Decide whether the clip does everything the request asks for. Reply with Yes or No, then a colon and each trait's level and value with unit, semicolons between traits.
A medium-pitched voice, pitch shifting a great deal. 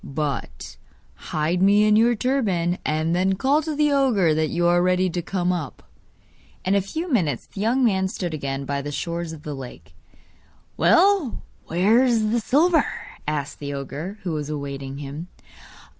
Yes: medium, 175 Hz; wide, 6.8 semitones